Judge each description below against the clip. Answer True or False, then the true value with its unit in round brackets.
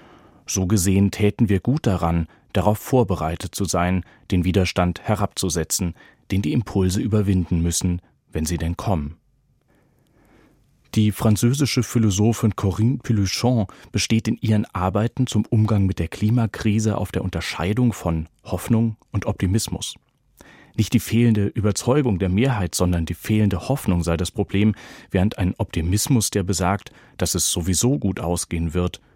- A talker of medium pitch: False (100 Hz)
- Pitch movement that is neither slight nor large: True (3.7 semitones)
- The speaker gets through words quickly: False (140 wpm)